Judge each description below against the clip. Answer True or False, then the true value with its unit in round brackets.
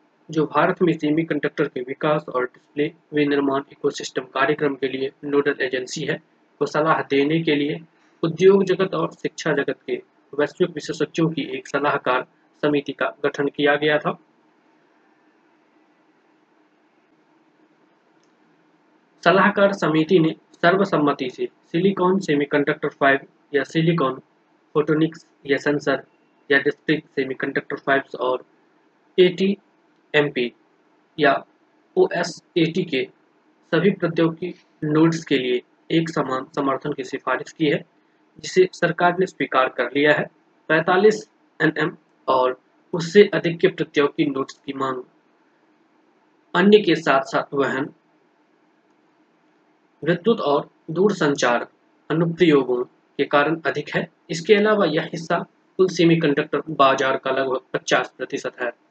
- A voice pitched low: False (160 Hz)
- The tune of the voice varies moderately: False (6.0 semitones)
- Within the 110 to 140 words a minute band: True (120 wpm)